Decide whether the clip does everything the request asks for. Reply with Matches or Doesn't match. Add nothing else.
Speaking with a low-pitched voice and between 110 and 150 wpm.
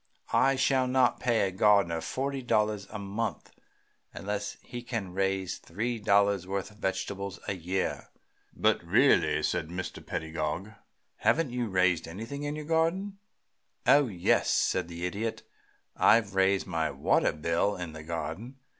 Matches